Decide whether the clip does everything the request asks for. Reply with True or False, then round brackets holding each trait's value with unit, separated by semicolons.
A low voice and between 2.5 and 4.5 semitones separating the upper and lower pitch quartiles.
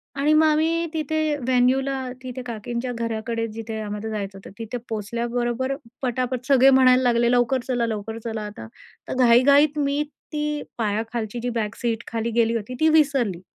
False (240 Hz; 2.9 semitones)